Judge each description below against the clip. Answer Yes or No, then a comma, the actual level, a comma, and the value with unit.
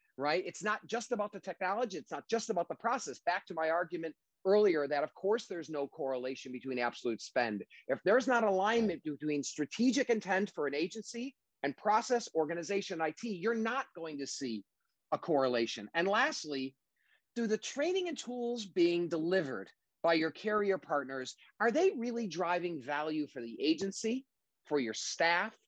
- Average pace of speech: Yes, average, 170 wpm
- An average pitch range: No, wide, 7.3 semitones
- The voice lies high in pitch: No, medium, 180 Hz